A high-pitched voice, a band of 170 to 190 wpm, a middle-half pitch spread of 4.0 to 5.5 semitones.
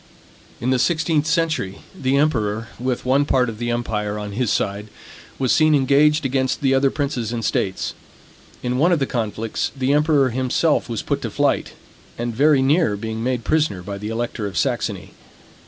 No: low, 125 Hz; average, 180 wpm; average, 4.3 semitones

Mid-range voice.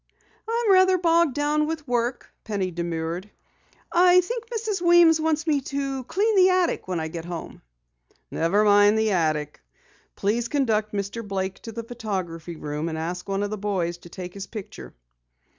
No: high, 215 Hz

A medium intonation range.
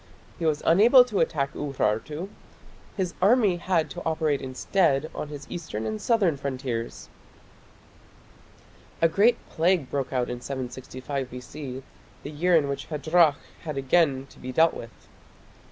Yes: average, 4.7 semitones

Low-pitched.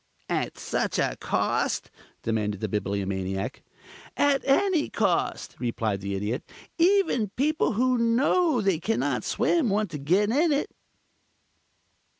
No: high, 205 Hz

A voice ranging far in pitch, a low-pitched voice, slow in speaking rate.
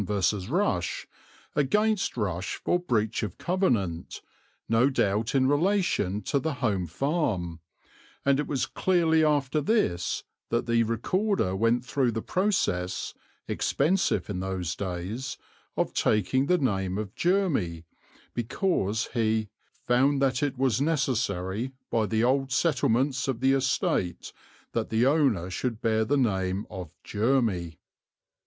Yes: wide, 6.2 semitones; low, 120 Hz; slow, 130 wpm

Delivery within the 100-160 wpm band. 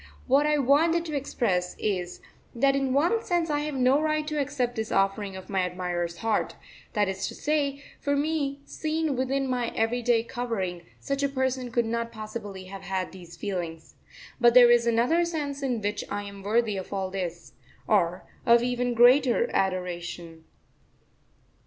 No: average, 170 wpm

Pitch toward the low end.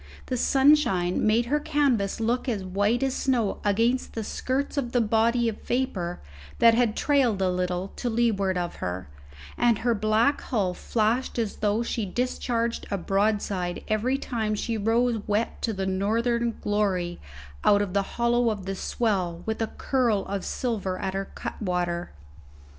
No: high, 220 Hz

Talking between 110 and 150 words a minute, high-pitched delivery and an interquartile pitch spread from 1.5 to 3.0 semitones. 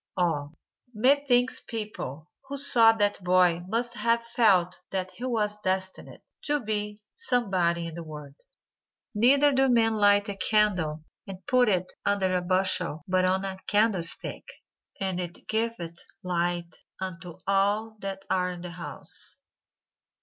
No: average, 140 wpm; high, 195 Hz; average, 4.0 semitones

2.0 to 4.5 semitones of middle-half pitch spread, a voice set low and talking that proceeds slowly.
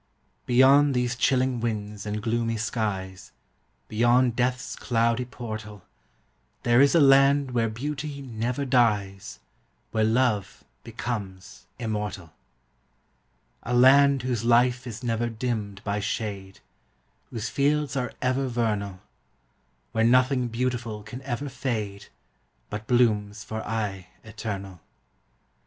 Yes: average, 3.2 semitones; low, 115 Hz; slow, 110 wpm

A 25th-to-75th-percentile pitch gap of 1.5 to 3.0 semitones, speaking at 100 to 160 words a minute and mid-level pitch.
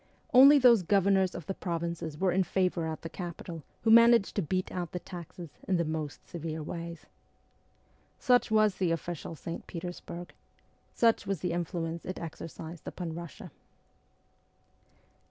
Yes: average, 2.7 semitones; average, 150 wpm; medium, 175 Hz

